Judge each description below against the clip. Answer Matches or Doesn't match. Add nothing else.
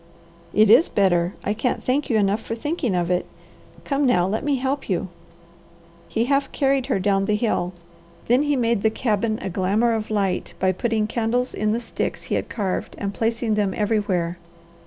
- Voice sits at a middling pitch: Doesn't match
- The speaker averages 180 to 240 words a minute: Matches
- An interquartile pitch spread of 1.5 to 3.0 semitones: Doesn't match